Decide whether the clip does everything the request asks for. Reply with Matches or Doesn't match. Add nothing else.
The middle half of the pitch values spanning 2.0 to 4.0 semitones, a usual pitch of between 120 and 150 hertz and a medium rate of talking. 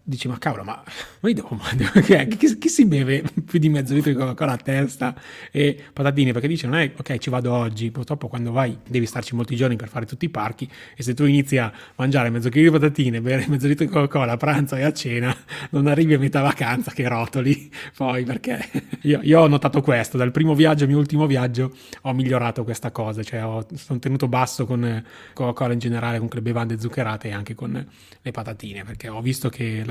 Doesn't match